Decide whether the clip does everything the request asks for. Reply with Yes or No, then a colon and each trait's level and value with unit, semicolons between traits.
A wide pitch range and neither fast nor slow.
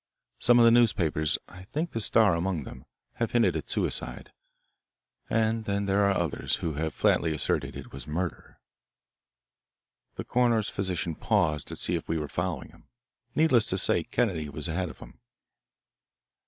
Yes: wide, 6.1 semitones; average, 165 wpm